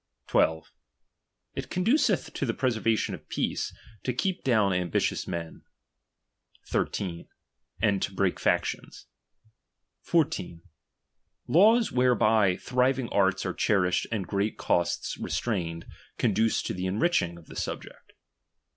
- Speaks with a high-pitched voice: No, low, 105 Hz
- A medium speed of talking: No, slow, 120 wpm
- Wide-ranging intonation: Yes, wide, 5.9 semitones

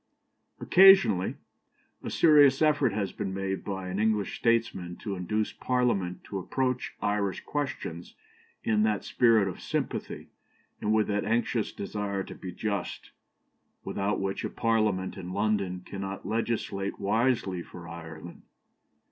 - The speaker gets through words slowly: Yes, slow, 130 wpm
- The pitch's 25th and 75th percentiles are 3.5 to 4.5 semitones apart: No, average, 3.1 semitones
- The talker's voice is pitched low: Yes, low, 100 Hz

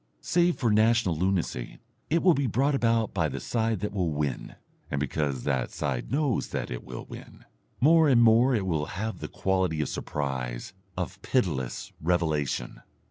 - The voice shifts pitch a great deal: Yes, wide, 8.4 semitones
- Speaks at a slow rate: No, average, 170 wpm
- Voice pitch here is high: No, very low, 95 Hz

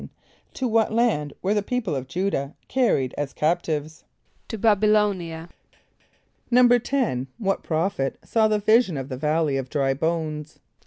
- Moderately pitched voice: Yes, medium, 170 Hz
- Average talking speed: Yes, average, 160 wpm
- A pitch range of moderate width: No, wide, 6.6 semitones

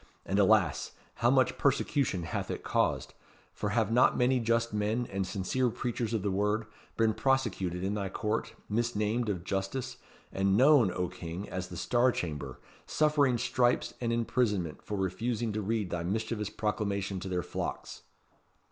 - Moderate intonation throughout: Yes, average, 3.8 semitones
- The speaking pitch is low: Yes, low, 105 Hz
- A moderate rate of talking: Yes, average, 160 wpm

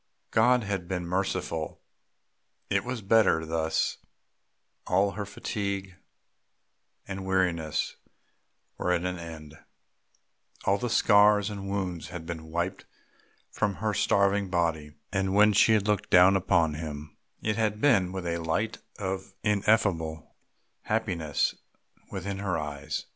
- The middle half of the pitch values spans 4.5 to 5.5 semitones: No, average, 3.5 semitones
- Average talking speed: No, slow, 125 wpm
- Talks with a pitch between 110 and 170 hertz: No, very low, 95 Hz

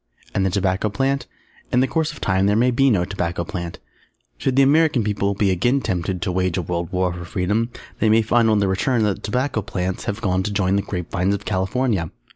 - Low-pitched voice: Yes, low, 100 Hz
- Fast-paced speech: Yes, fast, 235 wpm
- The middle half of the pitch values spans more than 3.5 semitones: Yes, average, 3.9 semitones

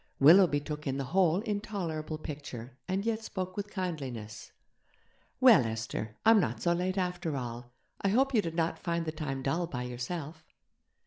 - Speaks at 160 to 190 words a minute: Yes, average, 170 wpm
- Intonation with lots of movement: Yes, wide, 5.7 semitones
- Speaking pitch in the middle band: Yes, medium, 165 Hz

